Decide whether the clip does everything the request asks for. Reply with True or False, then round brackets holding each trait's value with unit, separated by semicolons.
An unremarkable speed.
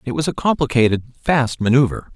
True (165 wpm)